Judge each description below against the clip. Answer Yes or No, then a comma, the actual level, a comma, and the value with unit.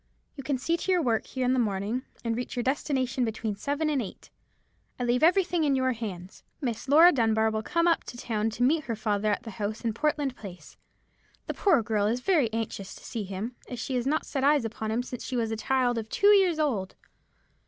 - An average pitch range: Yes, average, 4.5 semitones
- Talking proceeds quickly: Yes, fast, 230 wpm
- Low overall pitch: No, high, 245 Hz